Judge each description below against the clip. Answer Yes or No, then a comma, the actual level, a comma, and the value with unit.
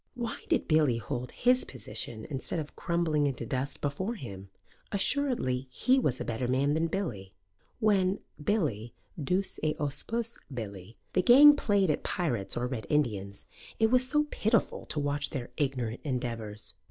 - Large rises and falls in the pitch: Yes, wide, 8.4 semitones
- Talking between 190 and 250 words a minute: No, average, 155 wpm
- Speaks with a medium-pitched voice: Yes, medium, 145 Hz